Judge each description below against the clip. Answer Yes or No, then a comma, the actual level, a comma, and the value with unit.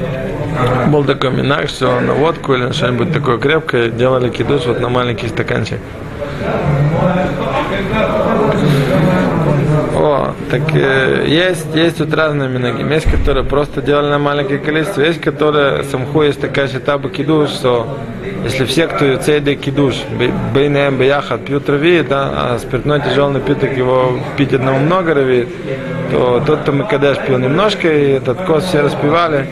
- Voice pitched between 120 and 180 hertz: Yes, medium, 140 Hz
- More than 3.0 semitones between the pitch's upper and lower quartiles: No, narrow, 2.6 semitones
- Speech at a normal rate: Yes, average, 150 wpm